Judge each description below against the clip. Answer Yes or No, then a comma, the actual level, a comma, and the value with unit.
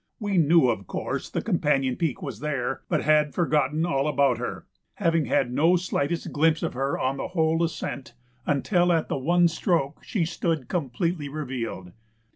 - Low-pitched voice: No, medium, 150 Hz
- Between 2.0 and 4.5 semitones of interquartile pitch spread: Yes, average, 3.7 semitones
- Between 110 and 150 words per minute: No, average, 170 wpm